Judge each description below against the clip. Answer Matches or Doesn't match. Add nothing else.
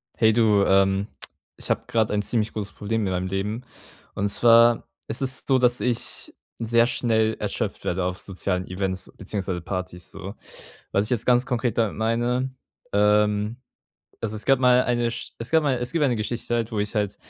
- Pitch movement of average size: Matches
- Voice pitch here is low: Matches